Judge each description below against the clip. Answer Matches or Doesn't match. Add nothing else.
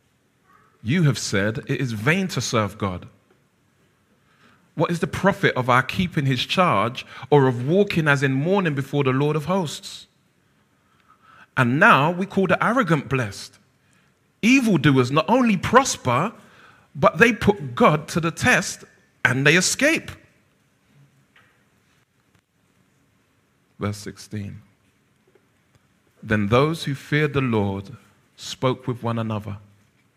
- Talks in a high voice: Doesn't match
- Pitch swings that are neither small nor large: Doesn't match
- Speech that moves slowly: Matches